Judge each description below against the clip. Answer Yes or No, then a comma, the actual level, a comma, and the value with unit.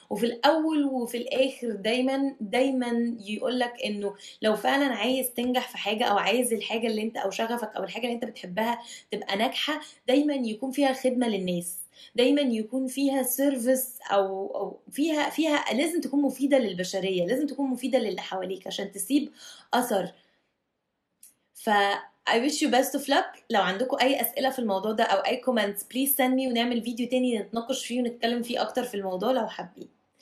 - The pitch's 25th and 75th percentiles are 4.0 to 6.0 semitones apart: No, average, 3.5 semitones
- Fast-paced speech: Yes, fast, 170 wpm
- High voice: Yes, high, 245 Hz